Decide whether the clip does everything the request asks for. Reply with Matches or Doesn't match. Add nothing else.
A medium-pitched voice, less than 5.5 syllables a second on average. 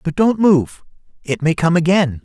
Matches